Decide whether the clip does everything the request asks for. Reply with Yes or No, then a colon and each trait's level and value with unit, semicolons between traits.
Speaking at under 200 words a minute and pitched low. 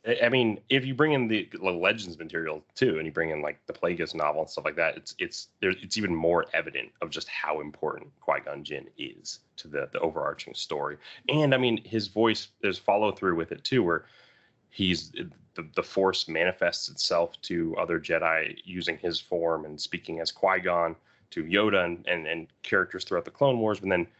No: fast, 205 wpm; low, 105 Hz